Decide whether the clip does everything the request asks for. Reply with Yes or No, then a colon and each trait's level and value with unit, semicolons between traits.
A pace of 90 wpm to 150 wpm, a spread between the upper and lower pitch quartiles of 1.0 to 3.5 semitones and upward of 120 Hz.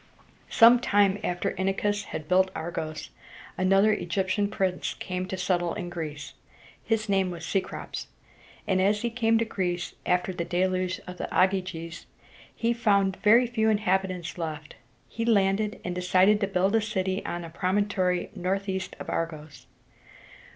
Yes: average, 145 wpm; narrow, 2.5 semitones; high, 190 Hz